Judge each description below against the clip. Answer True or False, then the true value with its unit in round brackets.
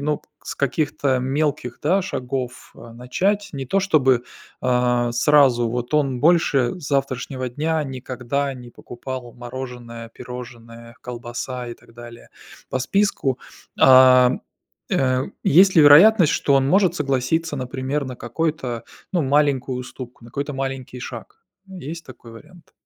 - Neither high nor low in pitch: False (130 Hz)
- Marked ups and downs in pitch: False (3.3 semitones)